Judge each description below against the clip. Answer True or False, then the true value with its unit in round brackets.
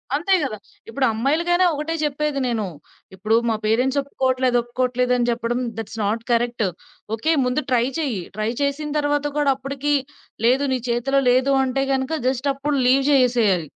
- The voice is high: True (255 Hz)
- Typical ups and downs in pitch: True (3.0 semitones)